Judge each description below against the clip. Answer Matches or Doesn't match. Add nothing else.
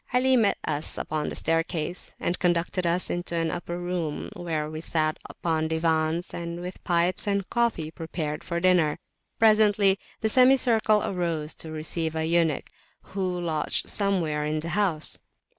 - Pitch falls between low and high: Matches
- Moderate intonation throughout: Matches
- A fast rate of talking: Doesn't match